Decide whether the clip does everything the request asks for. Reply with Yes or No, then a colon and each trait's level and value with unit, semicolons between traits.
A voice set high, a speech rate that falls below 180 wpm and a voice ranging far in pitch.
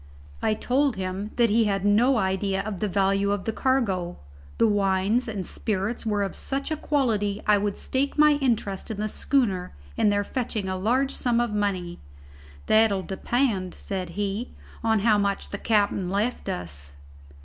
No: high, 205 Hz; average, 170 wpm; average, 3.2 semitones